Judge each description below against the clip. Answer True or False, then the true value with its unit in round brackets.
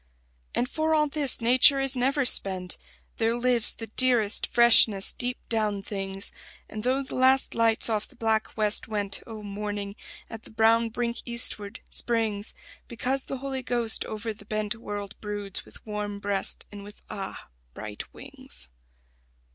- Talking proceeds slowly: False (155 wpm)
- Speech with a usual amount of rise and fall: True (3.1 semitones)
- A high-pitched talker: True (220 Hz)